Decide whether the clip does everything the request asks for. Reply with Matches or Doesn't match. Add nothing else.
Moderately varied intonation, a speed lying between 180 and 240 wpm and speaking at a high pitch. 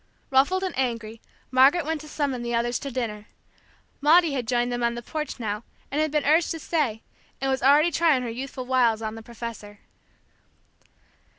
Matches